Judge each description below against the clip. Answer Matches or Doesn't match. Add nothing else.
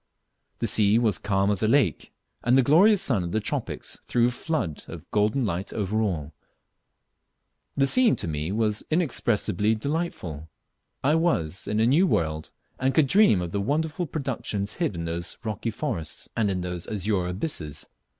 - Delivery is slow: Doesn't match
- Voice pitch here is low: Matches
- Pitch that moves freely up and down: Matches